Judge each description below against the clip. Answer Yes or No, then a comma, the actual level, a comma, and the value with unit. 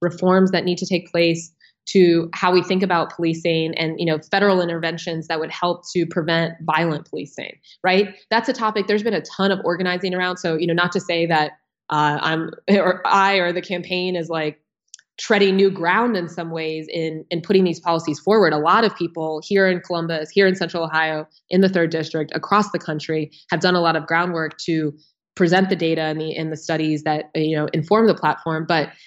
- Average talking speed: No, fast, 215 wpm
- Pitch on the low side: No, medium, 170 Hz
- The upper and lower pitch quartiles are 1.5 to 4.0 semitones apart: Yes, narrow, 2.5 semitones